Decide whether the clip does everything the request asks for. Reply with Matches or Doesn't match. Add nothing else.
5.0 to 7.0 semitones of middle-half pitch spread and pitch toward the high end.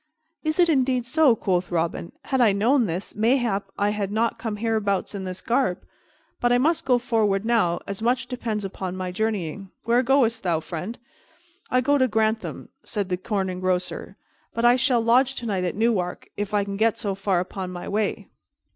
Doesn't match